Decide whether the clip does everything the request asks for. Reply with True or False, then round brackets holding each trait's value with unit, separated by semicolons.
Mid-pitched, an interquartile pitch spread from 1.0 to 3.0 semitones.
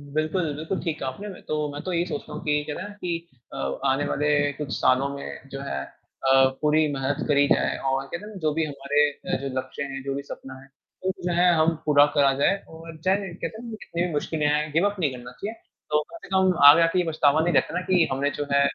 False (150 Hz; 3.8 semitones)